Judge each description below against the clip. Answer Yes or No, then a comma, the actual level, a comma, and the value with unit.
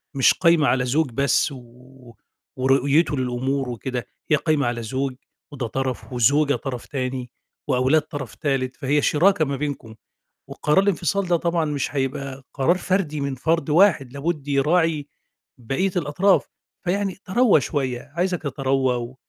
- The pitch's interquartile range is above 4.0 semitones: No, average, 3.7 semitones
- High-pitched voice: No, medium, 140 Hz